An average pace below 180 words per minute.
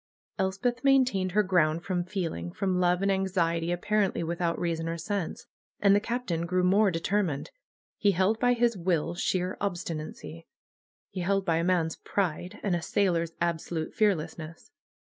Yes: average, 155 wpm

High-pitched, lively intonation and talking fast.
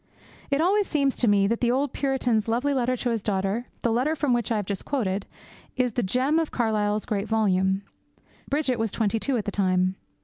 No: high, 230 Hz; average, 4.5 semitones; fast, 210 wpm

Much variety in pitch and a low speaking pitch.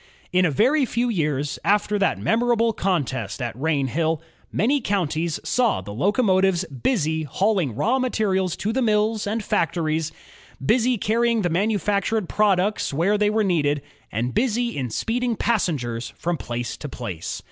No: wide, 6.7 semitones; high, 190 Hz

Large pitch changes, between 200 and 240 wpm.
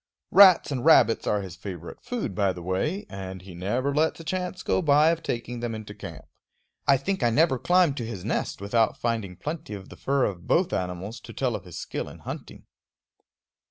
Yes: wide, 8.2 semitones; fast, 205 wpm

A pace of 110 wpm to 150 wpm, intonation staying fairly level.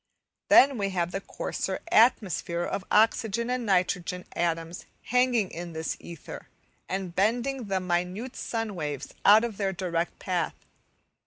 No: average, 140 wpm; average, 4.5 semitones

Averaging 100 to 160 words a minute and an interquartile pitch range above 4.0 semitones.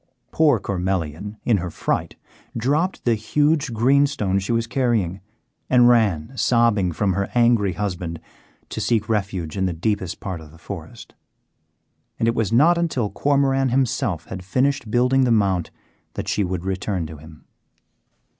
Yes: average, 155 wpm; average, 5.3 semitones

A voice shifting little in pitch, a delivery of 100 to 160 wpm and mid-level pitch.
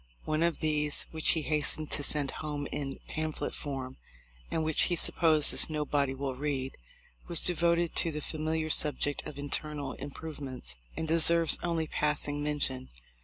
Yes: narrow, 1.8 semitones; average, 150 wpm; medium, 150 Hz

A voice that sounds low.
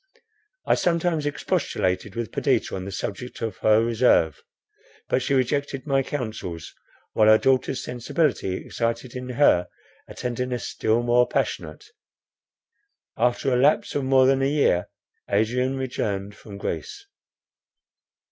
Yes: low, 125 Hz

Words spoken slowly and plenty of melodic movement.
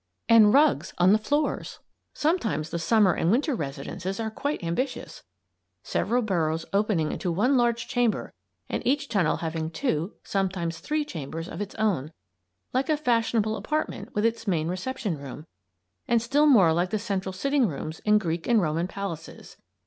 No: average, 165 wpm; wide, 6.3 semitones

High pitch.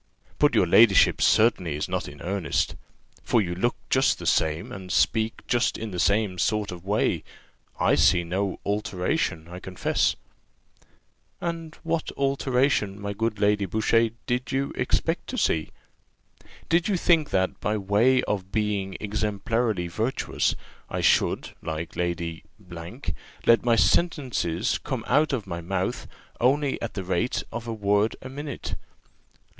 No: low, 105 Hz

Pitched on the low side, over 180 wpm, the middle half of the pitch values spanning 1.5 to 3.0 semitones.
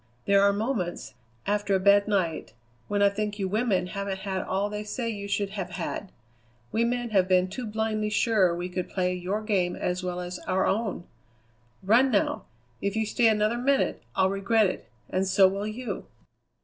No: high, 200 Hz; average, 190 wpm; narrow, 2.4 semitones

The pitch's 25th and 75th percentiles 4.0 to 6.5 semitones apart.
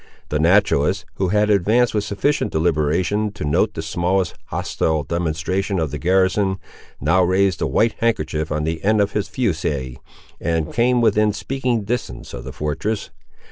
Yes: average, 5.0 semitones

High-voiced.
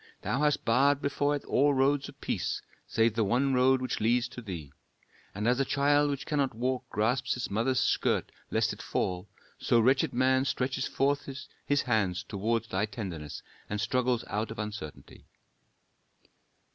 No: low, 125 Hz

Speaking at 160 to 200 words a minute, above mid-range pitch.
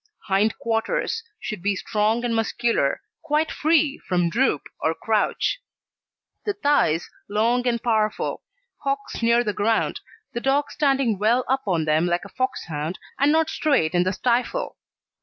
No: average, 150 wpm; high, 235 Hz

